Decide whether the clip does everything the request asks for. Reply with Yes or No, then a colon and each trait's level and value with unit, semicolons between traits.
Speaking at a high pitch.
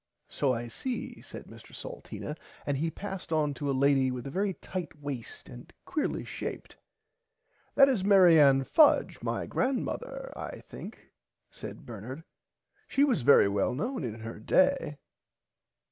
No: medium, 150 Hz